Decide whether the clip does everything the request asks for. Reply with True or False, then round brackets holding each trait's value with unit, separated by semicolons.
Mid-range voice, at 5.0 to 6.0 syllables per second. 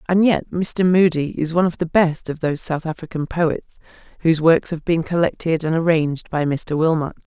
True (165 Hz; 5.5 syllables/s)